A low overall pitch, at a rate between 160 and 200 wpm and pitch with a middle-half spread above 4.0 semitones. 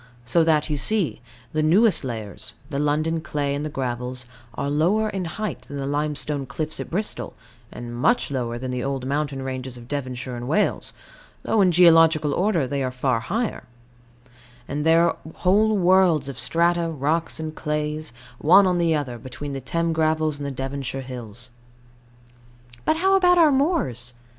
No: medium, 150 Hz; average, 170 wpm; average, 4.4 semitones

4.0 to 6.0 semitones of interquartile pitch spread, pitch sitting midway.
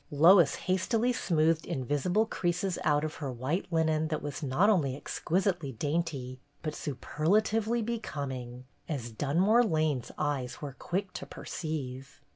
Yes: average, 5.0 semitones; medium, 155 Hz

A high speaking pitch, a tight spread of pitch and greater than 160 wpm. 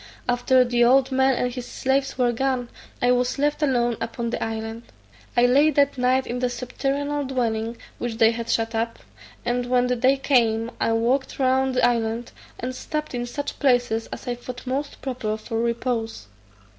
Yes: high, 245 Hz; narrow, 2.1 semitones; average, 180 wpm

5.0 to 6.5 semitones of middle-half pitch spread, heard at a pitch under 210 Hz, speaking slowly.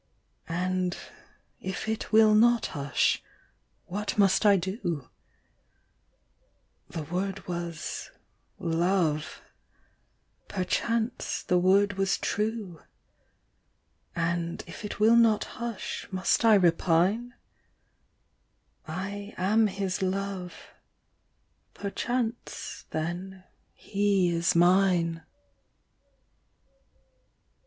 No: average, 3.2 semitones; high, 190 Hz; slow, 80 wpm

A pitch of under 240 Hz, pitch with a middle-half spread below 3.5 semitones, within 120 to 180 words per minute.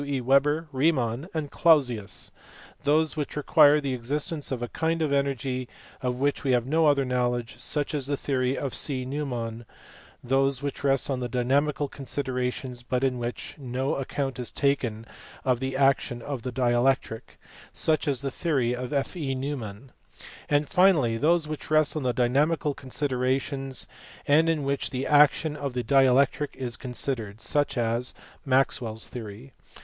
Yes: low, 135 Hz; average, 2.7 semitones; average, 160 wpm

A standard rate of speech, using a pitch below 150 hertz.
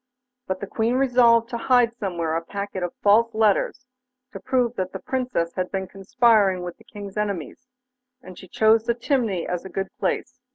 No: average, 190 wpm; high, 210 Hz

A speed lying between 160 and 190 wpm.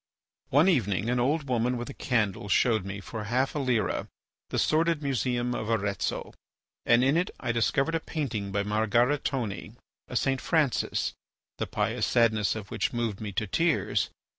Yes: average, 165 wpm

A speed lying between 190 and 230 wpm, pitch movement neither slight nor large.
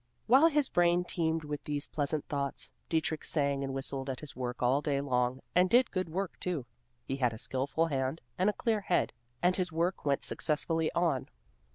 Yes: average, 195 wpm; average, 4.5 semitones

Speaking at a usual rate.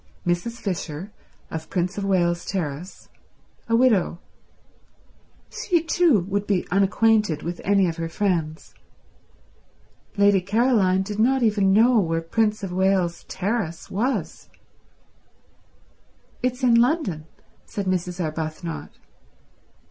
No: slow, 110 wpm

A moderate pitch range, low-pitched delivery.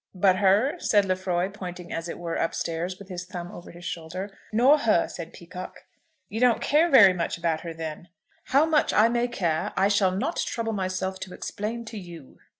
No: average, 4.0 semitones; medium, 185 Hz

